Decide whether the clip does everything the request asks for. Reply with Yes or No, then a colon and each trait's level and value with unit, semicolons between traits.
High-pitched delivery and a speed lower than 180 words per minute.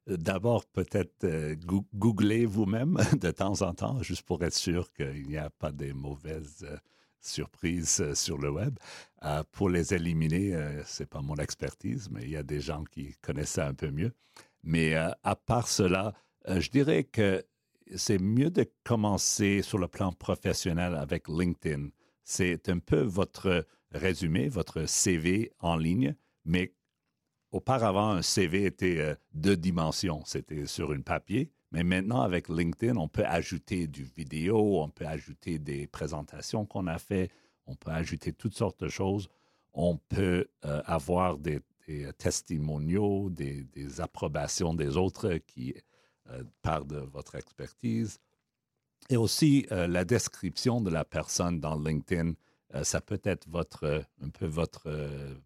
No: very low, 85 Hz; average, 160 wpm